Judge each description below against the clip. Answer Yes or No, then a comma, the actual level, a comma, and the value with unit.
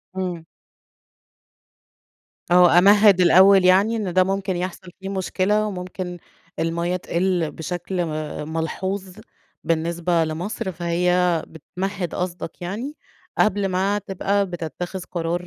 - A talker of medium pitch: Yes, medium, 180 Hz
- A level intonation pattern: Yes, narrow, 2.1 semitones